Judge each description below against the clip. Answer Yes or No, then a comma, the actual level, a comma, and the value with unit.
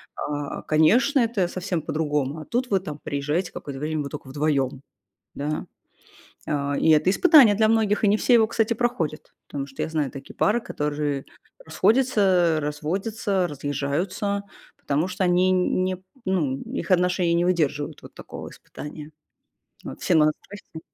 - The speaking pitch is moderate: Yes, medium, 170 Hz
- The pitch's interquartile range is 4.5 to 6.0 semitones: Yes, average, 5.2 semitones